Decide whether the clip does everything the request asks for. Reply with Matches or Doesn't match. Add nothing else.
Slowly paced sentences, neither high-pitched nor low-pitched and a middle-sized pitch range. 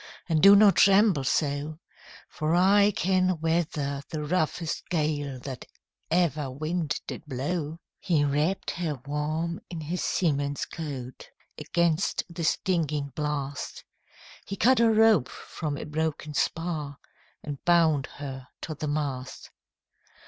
Matches